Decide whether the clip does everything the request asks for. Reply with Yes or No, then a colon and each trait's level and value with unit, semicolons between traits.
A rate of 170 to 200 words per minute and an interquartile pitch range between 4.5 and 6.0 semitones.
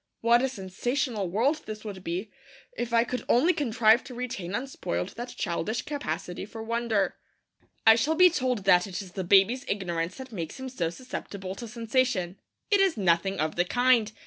Yes: average, 180 wpm; average, 5.0 semitones